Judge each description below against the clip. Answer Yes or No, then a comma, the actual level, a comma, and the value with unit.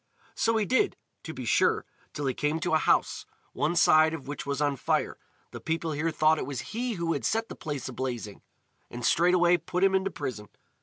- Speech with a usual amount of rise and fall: Yes, average, 4.1 semitones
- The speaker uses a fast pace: Yes, fast, 215 wpm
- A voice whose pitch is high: No, medium, 160 Hz